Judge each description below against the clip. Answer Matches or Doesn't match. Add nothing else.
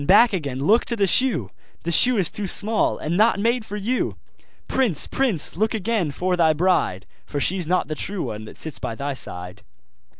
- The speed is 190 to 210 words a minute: Matches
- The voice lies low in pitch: Doesn't match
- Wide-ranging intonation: Matches